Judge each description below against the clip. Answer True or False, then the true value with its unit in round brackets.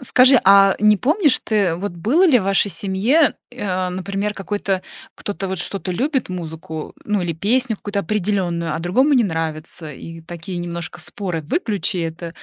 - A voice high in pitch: True (195 Hz)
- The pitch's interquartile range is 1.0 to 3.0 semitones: False (3.7 semitones)